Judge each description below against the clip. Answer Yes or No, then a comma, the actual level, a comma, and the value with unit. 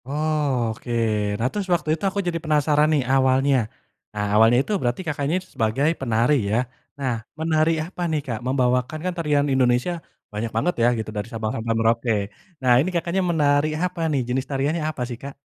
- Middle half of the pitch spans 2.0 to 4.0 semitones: No, average, 4.4 semitones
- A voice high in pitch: No, medium, 140 Hz